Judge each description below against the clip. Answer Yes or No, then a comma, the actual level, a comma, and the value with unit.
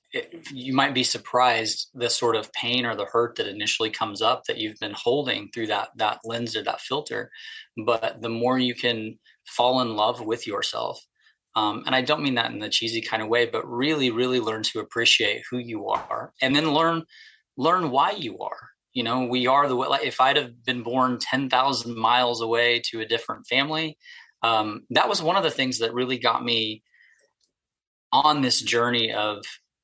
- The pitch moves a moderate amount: No, narrow, 2.2 semitones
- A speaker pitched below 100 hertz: No, low, 120 Hz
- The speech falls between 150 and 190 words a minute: No, average, 200 wpm